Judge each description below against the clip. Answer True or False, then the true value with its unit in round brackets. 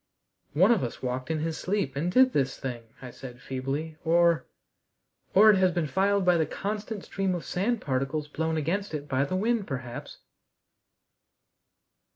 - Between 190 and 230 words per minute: False (170 wpm)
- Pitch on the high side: False (160 Hz)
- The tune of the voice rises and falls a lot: True (6.1 semitones)